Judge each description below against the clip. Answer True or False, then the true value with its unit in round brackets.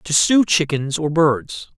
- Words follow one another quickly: False (170 wpm)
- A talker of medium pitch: True (155 Hz)